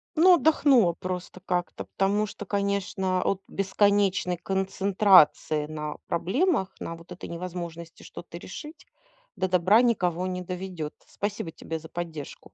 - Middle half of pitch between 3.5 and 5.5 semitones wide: No, average, 2.7 semitones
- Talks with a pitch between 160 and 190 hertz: Yes, medium, 185 Hz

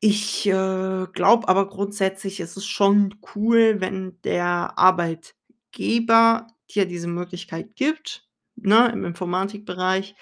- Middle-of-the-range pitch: No, high, 195 Hz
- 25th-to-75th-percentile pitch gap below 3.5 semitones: Yes, narrow, 2.4 semitones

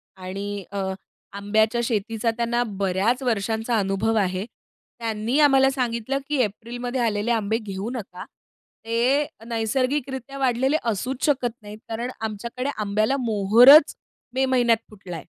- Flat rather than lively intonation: No, average, 3.4 semitones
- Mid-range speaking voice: No, high, 230 Hz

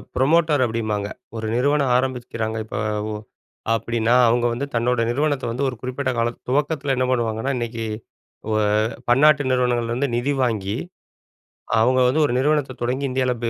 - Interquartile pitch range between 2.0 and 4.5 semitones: Yes, average, 3.0 semitones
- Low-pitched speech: Yes, low, 125 Hz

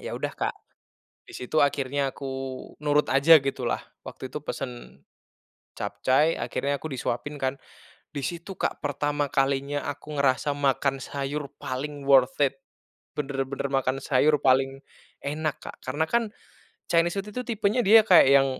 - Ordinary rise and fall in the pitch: No, narrow, 2.2 semitones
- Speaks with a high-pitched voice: No, medium, 140 Hz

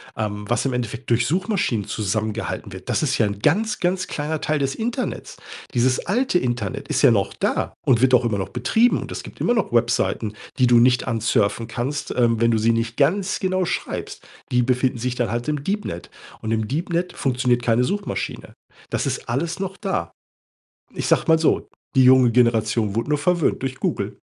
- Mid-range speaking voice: No, low, 125 Hz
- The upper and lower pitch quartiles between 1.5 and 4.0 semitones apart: No, wide, 5.9 semitones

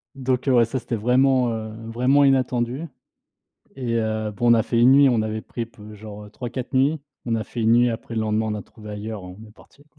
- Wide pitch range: No, average, 2.8 semitones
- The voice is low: Yes, low, 115 Hz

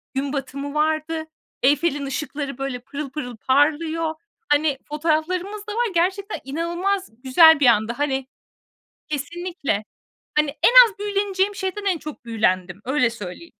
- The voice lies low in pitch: No, very high, 300 Hz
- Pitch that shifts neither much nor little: Yes, average, 4.4 semitones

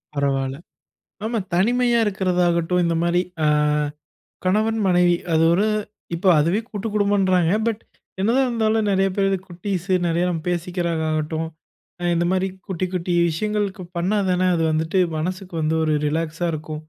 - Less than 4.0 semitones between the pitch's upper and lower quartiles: Yes, average, 3.5 semitones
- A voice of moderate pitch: Yes, medium, 180 Hz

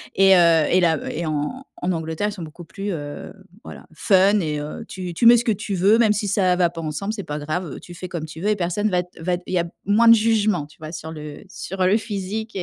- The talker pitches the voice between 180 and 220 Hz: Yes, medium, 185 Hz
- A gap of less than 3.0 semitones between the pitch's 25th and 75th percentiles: No, average, 4.3 semitones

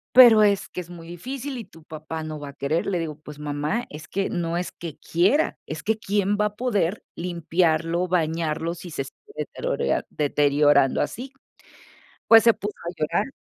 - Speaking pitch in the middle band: Yes, medium, 170 Hz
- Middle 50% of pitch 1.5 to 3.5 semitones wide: No, average, 5.1 semitones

